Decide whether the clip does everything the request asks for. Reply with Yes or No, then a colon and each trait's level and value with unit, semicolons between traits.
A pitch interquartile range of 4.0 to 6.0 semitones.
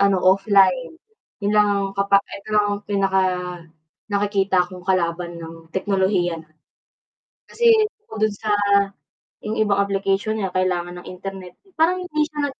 No: narrow, 2.4 semitones